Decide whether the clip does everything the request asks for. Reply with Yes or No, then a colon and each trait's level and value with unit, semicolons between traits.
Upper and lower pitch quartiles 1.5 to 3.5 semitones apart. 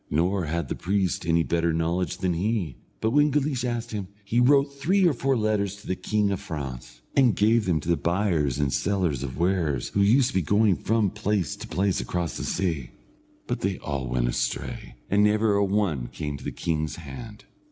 No: average, 5.1 semitones